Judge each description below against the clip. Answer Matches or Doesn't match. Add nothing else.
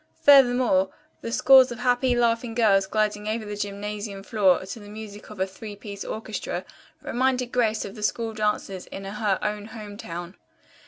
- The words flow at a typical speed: Matches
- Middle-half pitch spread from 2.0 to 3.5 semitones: Matches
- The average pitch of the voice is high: Matches